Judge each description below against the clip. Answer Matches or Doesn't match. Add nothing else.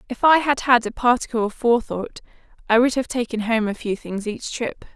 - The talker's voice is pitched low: Doesn't match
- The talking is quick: Matches